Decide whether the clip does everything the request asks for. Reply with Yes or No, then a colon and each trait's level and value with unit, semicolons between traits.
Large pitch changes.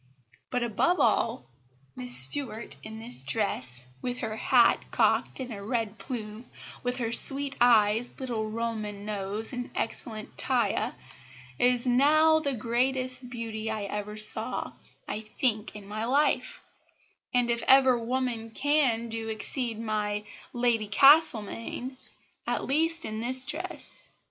No: average, 3.1 semitones